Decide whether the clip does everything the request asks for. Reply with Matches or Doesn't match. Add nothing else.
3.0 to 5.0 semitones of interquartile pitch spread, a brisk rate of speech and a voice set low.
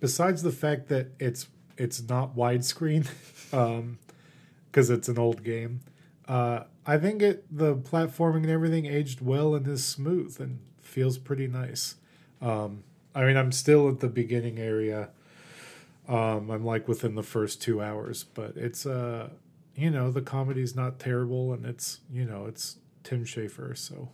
Doesn't match